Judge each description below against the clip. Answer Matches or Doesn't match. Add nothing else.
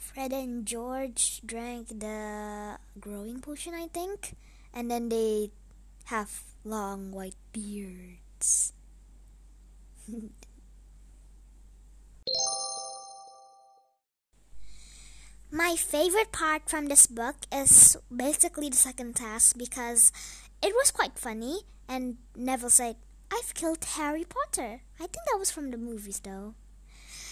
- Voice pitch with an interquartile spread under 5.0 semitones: Doesn't match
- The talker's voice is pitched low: Doesn't match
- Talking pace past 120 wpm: Doesn't match